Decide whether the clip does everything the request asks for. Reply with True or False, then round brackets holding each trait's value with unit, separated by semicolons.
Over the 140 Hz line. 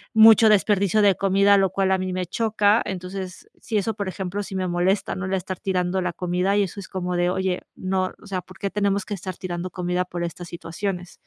True (190 Hz)